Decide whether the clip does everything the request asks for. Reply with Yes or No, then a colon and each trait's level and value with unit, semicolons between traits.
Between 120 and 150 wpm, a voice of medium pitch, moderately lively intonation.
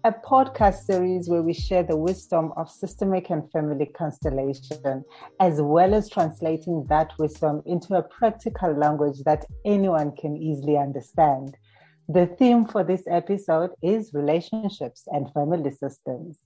Yes: average, 140 wpm; medium, 160 Hz; average, 3.9 semitones